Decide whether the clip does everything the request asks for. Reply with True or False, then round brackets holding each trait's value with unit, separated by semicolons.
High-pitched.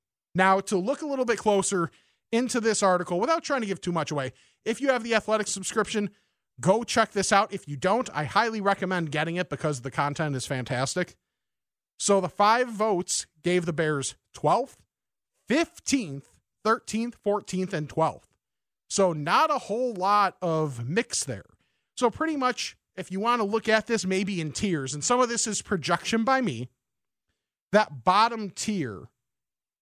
True (195 Hz)